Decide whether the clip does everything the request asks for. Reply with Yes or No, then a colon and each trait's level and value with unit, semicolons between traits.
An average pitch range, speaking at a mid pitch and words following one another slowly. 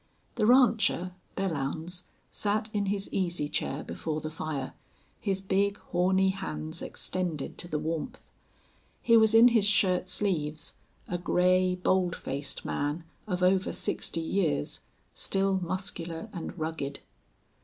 Yes: average, 3.5 semitones; medium, 180 Hz; slow, 130 wpm